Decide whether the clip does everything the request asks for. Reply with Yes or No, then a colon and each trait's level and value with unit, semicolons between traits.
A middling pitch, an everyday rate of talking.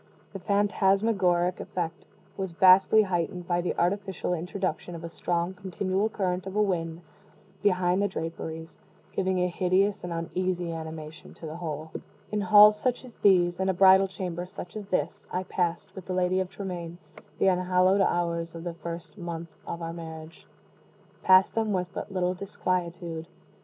Yes: medium, 180 Hz; average, 160 wpm